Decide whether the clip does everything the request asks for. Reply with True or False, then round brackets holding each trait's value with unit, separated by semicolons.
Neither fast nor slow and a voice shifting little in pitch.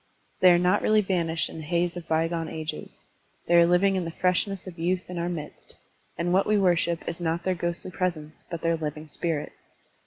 False (210 wpm; 1.8 semitones)